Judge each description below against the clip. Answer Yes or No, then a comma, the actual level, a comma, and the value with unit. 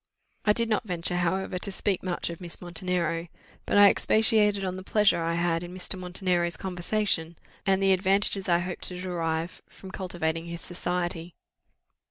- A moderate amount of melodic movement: No, narrow, 2.1 semitones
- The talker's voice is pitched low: No, medium, 180 Hz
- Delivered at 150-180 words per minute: Yes, average, 175 wpm